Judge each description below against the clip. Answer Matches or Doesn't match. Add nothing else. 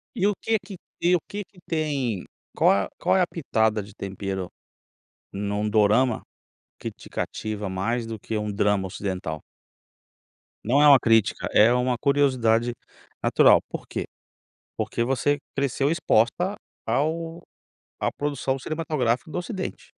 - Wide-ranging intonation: Matches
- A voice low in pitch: Matches